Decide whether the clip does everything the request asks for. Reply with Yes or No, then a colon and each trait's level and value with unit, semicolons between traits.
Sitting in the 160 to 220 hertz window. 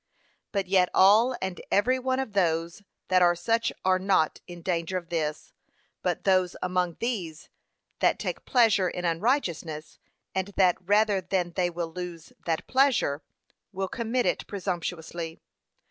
Yes: medium, 185 Hz